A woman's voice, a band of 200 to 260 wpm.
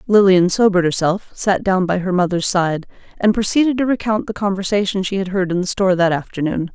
Yes: female; fast, 205 wpm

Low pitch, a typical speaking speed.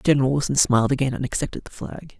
No: low, 130 Hz; fast, 220 wpm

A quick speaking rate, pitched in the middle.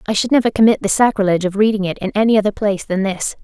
No: fast, 260 wpm; high, 205 Hz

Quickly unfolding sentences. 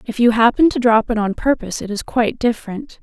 Yes: fast, 240 wpm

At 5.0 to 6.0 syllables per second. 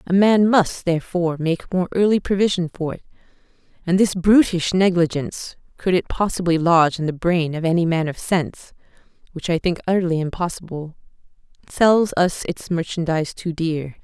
No: 4.7 syllables/s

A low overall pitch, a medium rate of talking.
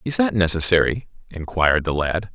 Yes: very low, 95 Hz; average, 155 wpm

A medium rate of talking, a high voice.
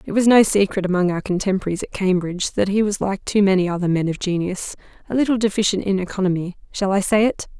No: fast, 215 wpm; high, 195 Hz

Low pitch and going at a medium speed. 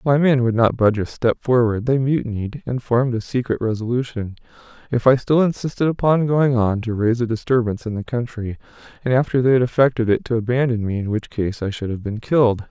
No: low, 120 Hz; fast, 210 wpm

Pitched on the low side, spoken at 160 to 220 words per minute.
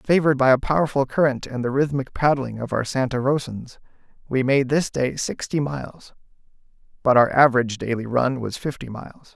Yes: low, 130 Hz; average, 175 wpm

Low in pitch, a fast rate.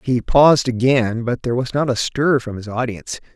Yes: low, 125 Hz; fast, 215 wpm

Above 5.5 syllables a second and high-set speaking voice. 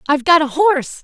Yes: 6.9 syllables/s; very high, 305 Hz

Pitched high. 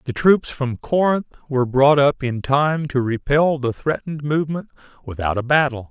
No: medium, 140 Hz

